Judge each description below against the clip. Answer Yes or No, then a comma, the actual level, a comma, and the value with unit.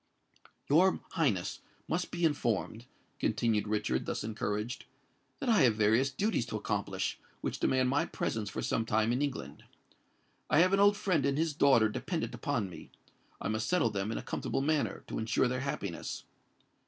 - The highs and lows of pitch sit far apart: Yes, wide, 6.3 semitones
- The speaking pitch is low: Yes, low, 125 Hz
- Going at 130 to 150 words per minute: No, average, 170 wpm